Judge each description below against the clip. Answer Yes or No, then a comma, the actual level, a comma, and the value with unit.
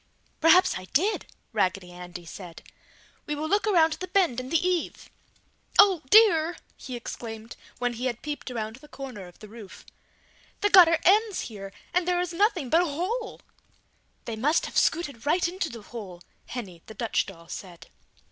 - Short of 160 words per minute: No, average, 175 wpm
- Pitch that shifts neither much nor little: No, wide, 8.5 semitones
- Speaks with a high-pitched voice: Yes, very high, 280 Hz